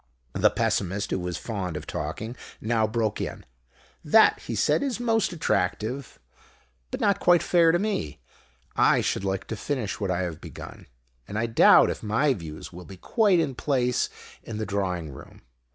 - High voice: No, low, 110 Hz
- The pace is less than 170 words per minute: No, average, 175 wpm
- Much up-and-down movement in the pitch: Yes, wide, 7.8 semitones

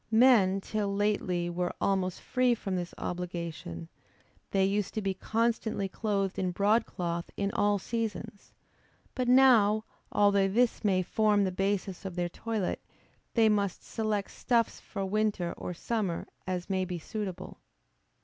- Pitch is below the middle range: No, high, 200 Hz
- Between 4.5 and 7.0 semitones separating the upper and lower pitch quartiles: No, average, 2.8 semitones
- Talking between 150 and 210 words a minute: No, average, 140 wpm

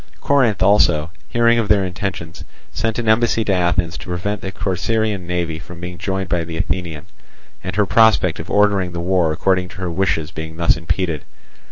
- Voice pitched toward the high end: No, very low, 90 Hz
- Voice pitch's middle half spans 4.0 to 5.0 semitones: No, average, 3.3 semitones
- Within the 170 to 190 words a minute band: Yes, average, 180 wpm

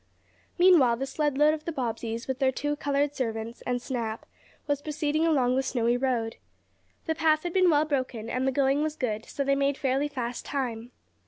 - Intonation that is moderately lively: Yes, average, 3.3 semitones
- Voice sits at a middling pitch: No, very high, 270 Hz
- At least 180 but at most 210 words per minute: Yes, average, 195 wpm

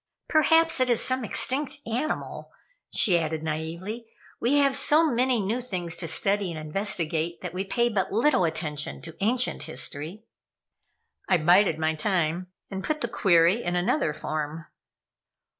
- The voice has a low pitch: No, high, 190 Hz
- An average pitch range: No, wide, 6.6 semitones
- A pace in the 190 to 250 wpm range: No, average, 150 wpm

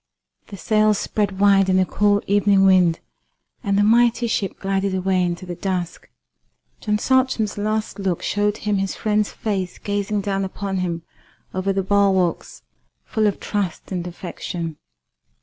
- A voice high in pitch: Yes, high, 195 Hz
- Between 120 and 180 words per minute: Yes, average, 150 wpm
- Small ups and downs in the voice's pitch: Yes, narrow, 1.9 semitones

